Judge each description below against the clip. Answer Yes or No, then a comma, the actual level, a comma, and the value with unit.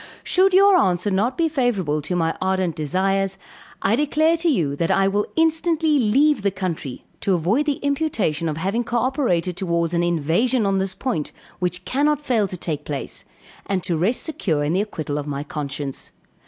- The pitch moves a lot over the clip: Yes, wide, 7.8 semitones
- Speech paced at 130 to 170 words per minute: No, average, 180 wpm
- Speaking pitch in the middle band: No, high, 195 Hz